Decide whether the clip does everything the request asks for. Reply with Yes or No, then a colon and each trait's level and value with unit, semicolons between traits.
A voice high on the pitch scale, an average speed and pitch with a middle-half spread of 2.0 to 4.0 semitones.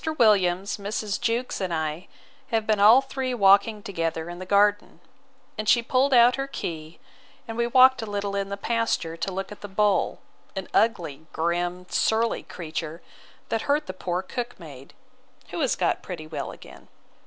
No: high, 200 Hz; average, 175 wpm; average, 4.7 semitones